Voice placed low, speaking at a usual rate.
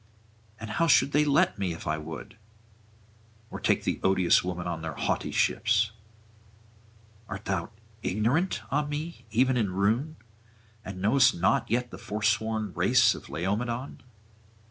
Yes: low, 110 Hz; average, 145 wpm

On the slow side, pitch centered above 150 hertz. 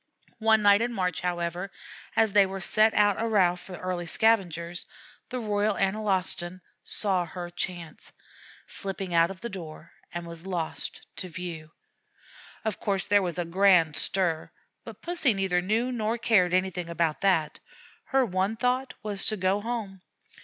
No: average, 160 wpm; high, 190 Hz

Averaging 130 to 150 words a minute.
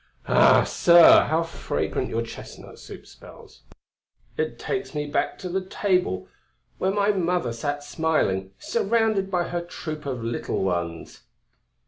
Yes: slow, 135 wpm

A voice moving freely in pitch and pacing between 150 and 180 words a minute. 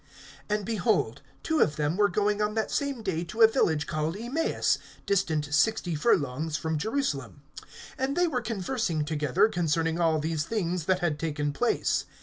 Yes: wide, 6.3 semitones; average, 165 wpm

